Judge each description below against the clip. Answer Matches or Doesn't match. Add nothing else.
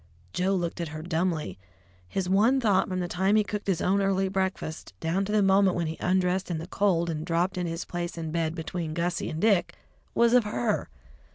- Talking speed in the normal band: Doesn't match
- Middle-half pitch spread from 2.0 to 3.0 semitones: Matches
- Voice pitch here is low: Doesn't match